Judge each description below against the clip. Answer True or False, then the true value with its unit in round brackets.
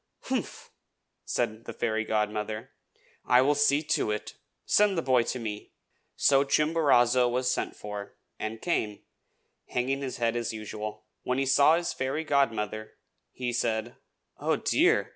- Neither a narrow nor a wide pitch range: True (4.1 semitones)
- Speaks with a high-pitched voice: False (120 Hz)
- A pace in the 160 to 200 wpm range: False (145 wpm)